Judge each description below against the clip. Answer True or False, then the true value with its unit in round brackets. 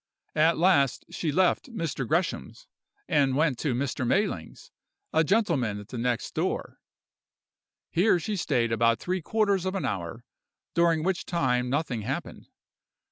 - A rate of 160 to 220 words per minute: False (140 wpm)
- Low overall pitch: False (155 Hz)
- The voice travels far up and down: True (6.5 semitones)